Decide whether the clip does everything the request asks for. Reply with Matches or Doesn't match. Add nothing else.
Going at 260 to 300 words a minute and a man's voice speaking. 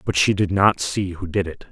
Matches